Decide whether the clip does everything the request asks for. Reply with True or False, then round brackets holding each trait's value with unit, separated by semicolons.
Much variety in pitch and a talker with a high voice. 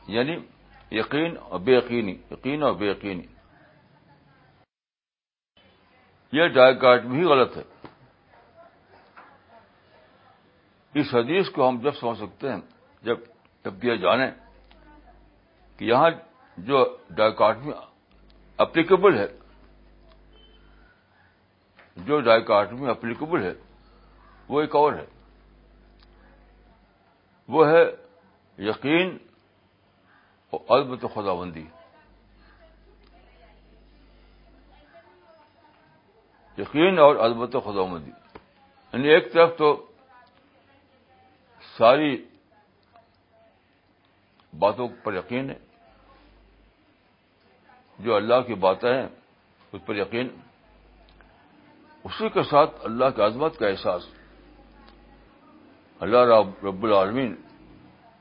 False (6.8 semitones; 115 Hz)